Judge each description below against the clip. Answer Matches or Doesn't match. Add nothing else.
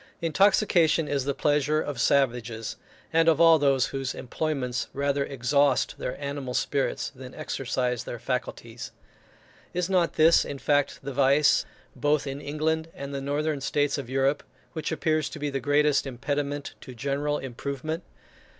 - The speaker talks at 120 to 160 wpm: Matches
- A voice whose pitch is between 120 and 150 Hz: Matches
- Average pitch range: Doesn't match